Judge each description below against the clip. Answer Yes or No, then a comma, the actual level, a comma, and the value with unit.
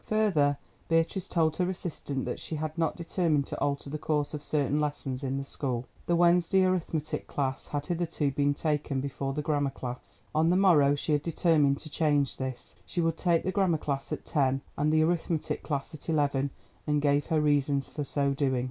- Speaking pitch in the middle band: Yes, medium, 150 Hz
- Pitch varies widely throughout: No, average, 2.8 semitones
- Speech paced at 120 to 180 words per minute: No, average, 195 wpm